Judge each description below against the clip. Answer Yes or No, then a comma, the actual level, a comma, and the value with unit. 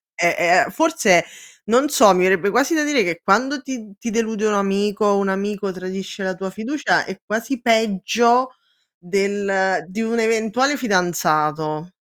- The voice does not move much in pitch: No, average, 3.7 semitones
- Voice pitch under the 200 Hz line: No, high, 205 Hz